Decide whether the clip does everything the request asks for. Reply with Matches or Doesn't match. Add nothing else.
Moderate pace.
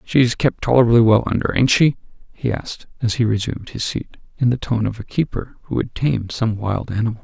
Doesn't match